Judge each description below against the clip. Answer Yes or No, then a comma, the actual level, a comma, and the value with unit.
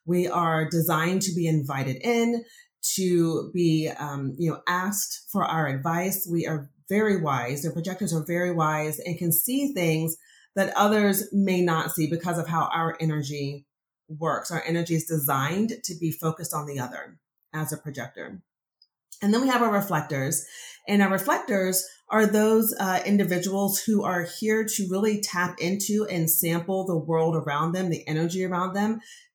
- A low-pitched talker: No, medium, 175 Hz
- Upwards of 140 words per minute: Yes, average, 170 wpm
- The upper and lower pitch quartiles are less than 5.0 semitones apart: Yes, average, 3.8 semitones